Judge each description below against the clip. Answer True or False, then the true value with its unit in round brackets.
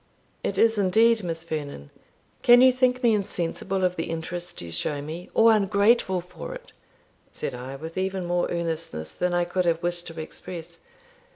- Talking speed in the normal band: True (175 wpm)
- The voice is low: False (175 Hz)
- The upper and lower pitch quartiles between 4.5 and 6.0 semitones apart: False (3.6 semitones)